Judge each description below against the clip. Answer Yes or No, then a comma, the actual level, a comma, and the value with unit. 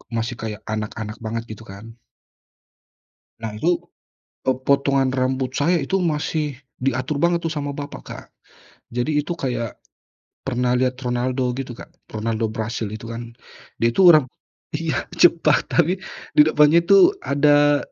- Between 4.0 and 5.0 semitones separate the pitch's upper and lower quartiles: Yes, average, 4.5 semitones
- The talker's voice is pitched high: No, low, 130 Hz